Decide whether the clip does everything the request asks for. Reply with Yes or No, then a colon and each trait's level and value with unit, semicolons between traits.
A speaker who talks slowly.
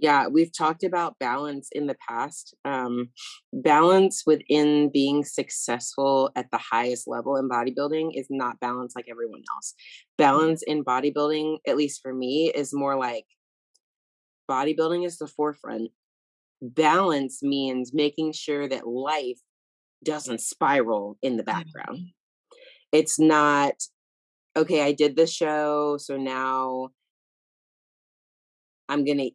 Yes: slow, 125 wpm